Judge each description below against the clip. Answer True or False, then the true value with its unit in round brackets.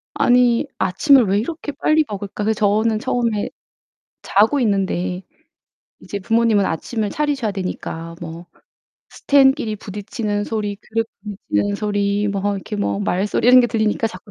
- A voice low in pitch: False (210 Hz)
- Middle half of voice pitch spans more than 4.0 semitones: False (2.7 semitones)